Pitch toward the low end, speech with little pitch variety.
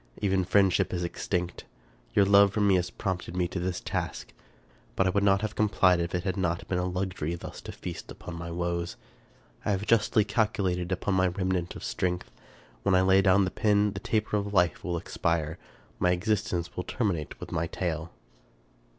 Yes: very low, 95 Hz; narrow, 2.3 semitones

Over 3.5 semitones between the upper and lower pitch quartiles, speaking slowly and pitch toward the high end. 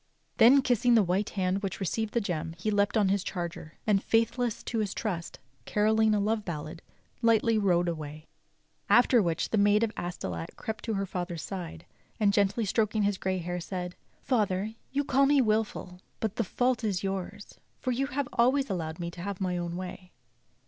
No: average, 4.0 semitones; average, 190 wpm; high, 200 Hz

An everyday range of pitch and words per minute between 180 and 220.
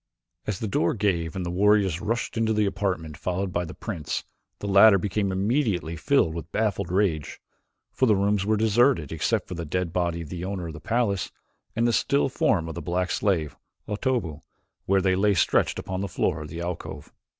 Yes: average, 3.7 semitones; average, 200 wpm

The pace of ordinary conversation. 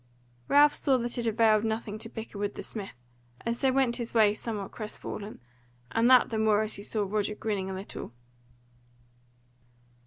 Yes: average, 175 wpm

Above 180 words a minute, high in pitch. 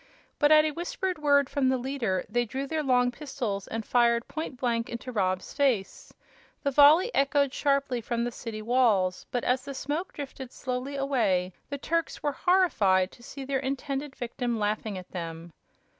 No: average, 175 wpm; very high, 260 Hz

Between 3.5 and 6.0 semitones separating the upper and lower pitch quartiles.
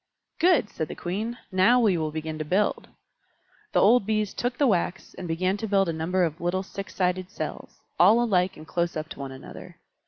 Yes: average, 4.2 semitones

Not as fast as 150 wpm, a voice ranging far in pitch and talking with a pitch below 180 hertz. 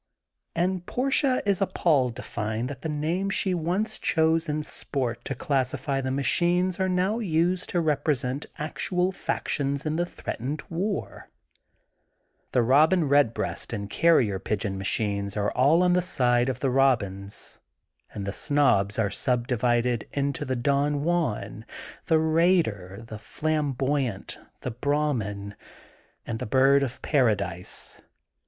Yes: average, 140 wpm; wide, 5.9 semitones; medium, 140 Hz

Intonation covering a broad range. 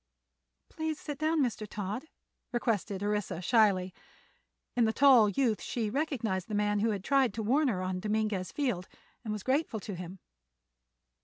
No: average, 4.4 semitones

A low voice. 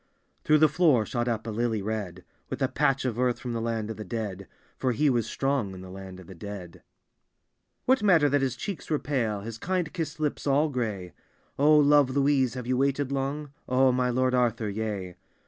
Yes: low, 125 Hz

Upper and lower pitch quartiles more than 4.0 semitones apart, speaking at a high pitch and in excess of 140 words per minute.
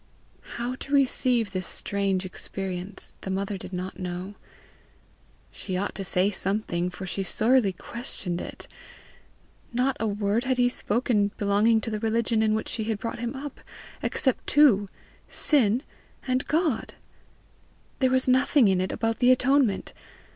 Yes: average, 4.5 semitones; high, 220 Hz; average, 150 wpm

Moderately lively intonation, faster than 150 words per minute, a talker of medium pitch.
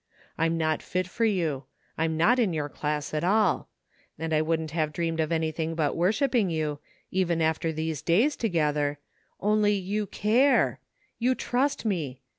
Yes: average, 4.7 semitones; average, 170 wpm; medium, 165 Hz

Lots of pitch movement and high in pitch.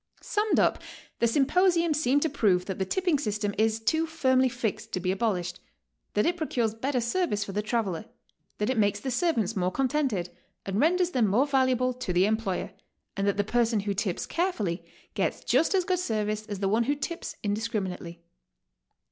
Yes: wide, 6.1 semitones; high, 225 Hz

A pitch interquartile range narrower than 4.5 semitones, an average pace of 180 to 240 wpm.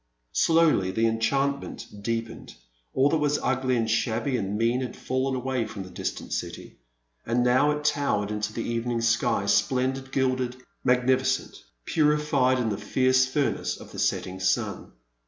No: average, 2.8 semitones; average, 155 wpm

